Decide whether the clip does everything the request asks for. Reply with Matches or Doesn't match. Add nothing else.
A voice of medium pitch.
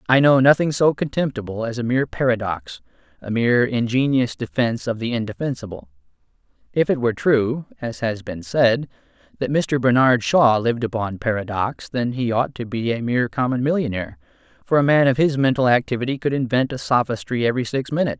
Doesn't match